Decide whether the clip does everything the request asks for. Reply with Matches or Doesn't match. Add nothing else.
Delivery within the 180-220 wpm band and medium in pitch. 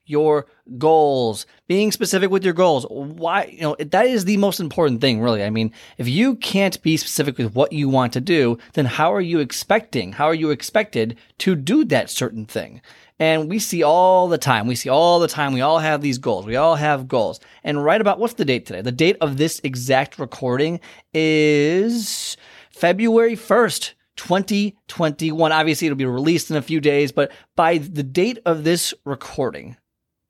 Matches